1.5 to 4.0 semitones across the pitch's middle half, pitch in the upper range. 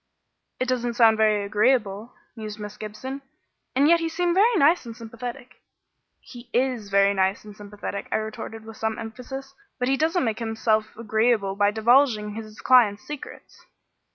Yes: average, 3.4 semitones; high, 225 Hz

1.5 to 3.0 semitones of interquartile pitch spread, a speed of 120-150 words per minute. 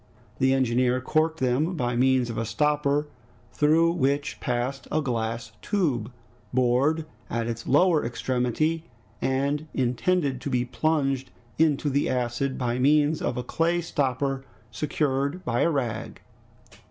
No: average, 3.6 semitones; slow, 135 wpm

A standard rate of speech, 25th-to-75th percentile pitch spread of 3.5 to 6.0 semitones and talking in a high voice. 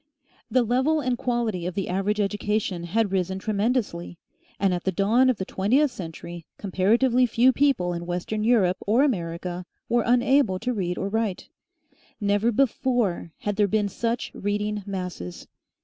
Yes: average, 155 wpm; average, 4.6 semitones; high, 205 Hz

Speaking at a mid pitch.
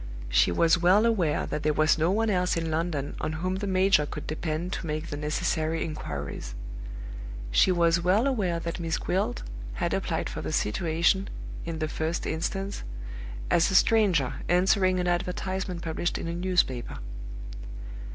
Yes: medium, 170 Hz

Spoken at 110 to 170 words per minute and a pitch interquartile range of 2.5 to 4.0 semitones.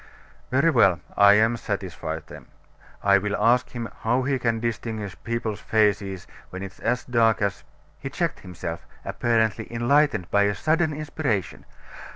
Yes: average, 160 wpm; average, 3.7 semitones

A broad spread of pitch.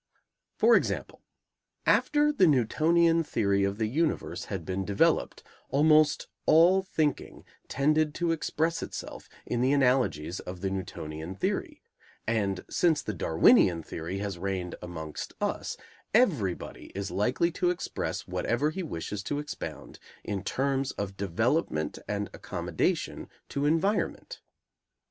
Yes: wide, 8.5 semitones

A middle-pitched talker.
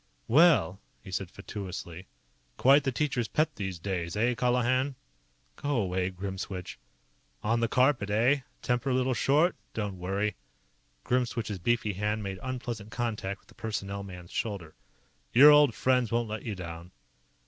No: low, 110 Hz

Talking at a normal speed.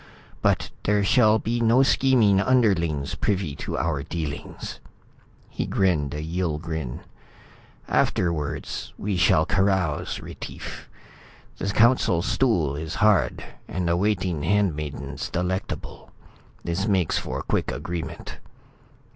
No: slow, 115 wpm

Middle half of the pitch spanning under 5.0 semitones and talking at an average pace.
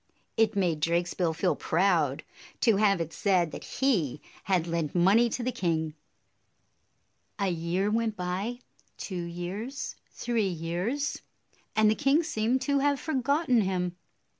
No: wide, 5.5 semitones; average, 145 wpm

